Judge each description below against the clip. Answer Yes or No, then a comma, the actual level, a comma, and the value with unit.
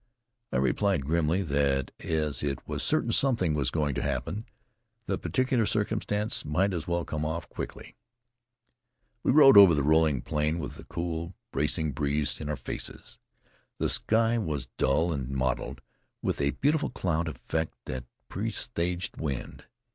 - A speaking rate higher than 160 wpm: No, average, 150 wpm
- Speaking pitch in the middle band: No, very low, 80 Hz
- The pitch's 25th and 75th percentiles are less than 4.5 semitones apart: No, average, 4.8 semitones